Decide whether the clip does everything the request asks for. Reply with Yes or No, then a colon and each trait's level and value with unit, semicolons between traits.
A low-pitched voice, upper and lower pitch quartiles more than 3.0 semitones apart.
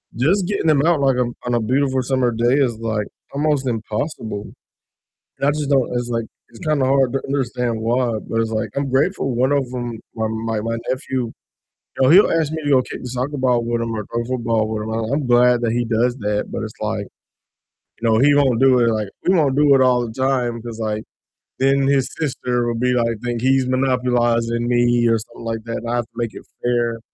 No: low, 125 Hz; narrow, 2.6 semitones